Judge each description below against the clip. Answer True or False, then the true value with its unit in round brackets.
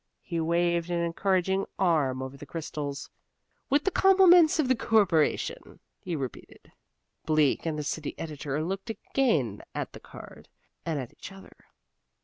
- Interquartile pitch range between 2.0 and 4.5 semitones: False (5.0 semitones)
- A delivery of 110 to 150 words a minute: True (145 wpm)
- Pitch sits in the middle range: True (170 Hz)